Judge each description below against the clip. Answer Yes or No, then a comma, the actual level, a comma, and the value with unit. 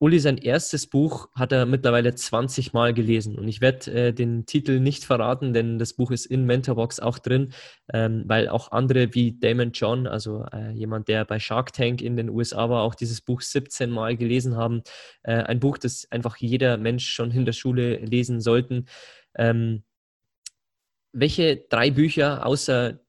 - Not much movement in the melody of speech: Yes, narrow, 1.9 semitones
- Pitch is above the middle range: No, low, 120 Hz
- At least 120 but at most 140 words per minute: No, average, 180 wpm